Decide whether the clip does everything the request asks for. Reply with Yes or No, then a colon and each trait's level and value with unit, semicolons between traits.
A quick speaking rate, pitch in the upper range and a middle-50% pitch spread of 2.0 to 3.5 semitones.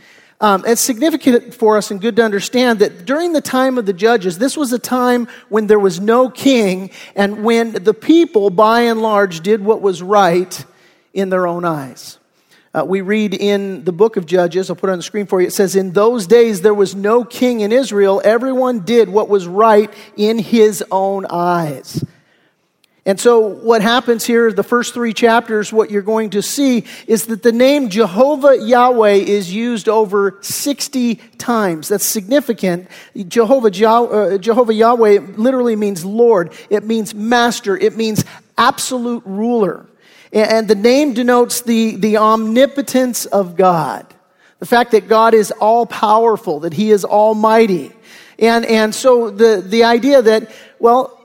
No: average, 170 wpm; high, 220 Hz; average, 2.9 semitones